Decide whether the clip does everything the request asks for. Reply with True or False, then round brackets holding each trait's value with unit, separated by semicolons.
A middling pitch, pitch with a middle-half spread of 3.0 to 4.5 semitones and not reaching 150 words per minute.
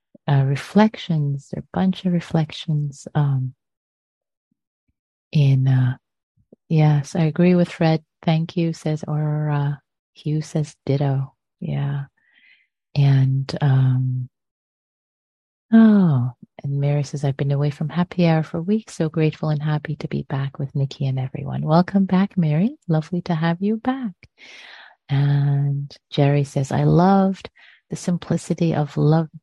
True (150 Hz; 3.5 semitones; 135 wpm)